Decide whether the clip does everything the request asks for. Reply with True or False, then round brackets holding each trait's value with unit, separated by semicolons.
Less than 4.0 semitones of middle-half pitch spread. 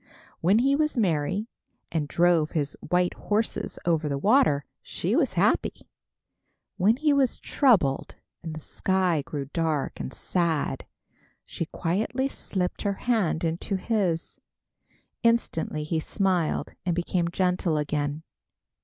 False (5.0 semitones)